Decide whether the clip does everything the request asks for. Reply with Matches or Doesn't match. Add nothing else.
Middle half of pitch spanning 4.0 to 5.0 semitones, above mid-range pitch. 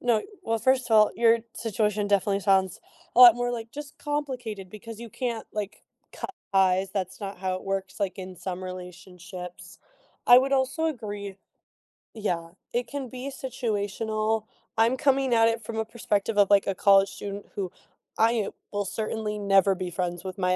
Doesn't match